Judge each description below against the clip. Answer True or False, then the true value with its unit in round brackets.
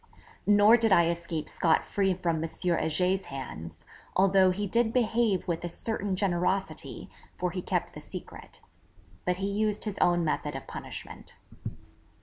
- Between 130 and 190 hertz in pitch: True (185 Hz)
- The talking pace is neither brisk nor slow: True (150 wpm)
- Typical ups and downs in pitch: True (3.2 semitones)